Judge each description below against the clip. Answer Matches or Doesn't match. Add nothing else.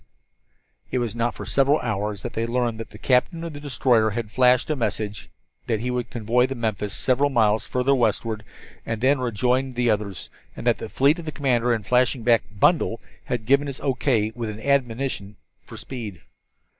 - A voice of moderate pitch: Doesn't match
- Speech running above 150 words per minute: Matches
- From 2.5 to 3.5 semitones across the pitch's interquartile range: Matches